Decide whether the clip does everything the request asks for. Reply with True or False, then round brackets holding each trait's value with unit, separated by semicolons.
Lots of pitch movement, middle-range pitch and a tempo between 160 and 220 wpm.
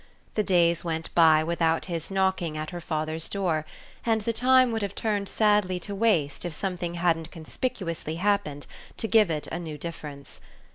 False (4.0 semitones; 175 Hz; 175 wpm)